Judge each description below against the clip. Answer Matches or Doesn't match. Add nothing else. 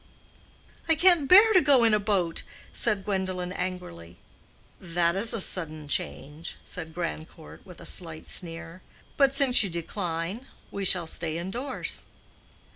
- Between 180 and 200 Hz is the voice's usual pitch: Matches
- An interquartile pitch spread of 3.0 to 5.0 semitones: Doesn't match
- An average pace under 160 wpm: Matches